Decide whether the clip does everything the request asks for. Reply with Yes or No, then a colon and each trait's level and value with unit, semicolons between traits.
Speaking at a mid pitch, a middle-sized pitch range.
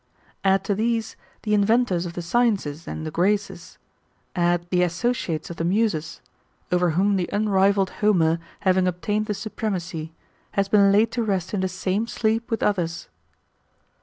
No: high, 195 Hz; average, 3.4 semitones